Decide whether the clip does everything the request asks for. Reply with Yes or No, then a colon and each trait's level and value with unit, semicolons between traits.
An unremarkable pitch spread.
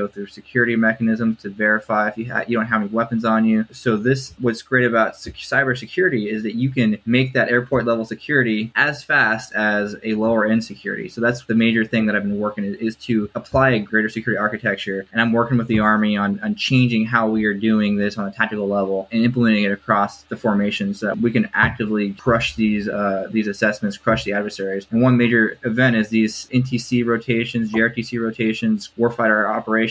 No: narrow, 1.9 semitones